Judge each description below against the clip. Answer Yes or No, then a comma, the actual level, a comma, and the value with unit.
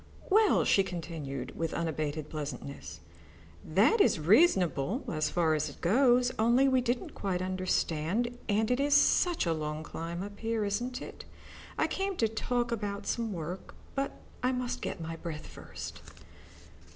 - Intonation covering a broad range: Yes, wide, 7.1 semitones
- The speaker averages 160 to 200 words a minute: No, average, 150 wpm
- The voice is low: No, high, 200 Hz